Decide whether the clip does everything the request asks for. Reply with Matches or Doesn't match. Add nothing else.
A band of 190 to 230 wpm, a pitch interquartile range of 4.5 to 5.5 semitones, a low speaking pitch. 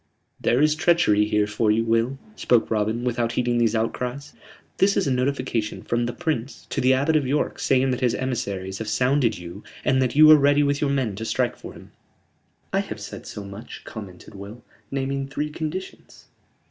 Doesn't match